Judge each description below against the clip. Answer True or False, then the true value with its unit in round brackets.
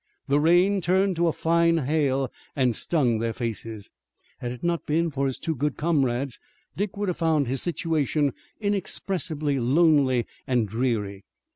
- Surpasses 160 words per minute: False (155 wpm)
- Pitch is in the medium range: True (145 Hz)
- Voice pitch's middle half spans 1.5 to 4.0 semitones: False (5.0 semitones)